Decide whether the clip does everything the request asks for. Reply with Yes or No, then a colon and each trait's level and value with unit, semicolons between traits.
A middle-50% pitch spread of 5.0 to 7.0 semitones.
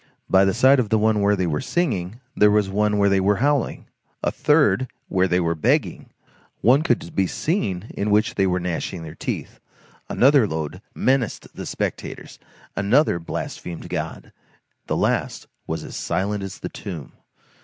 Yes: average, 5.3 semitones